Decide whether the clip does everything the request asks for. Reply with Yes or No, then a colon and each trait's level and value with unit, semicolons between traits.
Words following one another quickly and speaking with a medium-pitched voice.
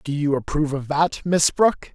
Yes: fast, 215 wpm; medium, 155 Hz